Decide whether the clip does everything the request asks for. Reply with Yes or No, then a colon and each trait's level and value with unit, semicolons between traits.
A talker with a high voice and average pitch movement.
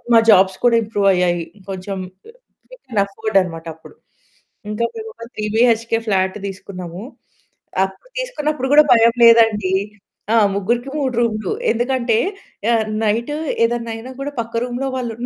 Yes: high, 225 Hz; average, 3.7 semitones